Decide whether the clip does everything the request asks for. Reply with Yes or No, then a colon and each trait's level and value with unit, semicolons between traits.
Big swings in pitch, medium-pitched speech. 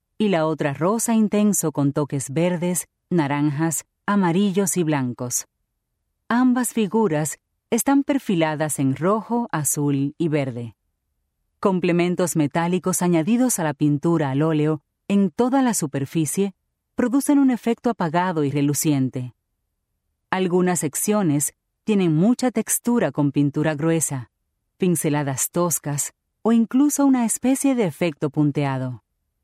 Yes: wide, 6.4 semitones; medium, 165 Hz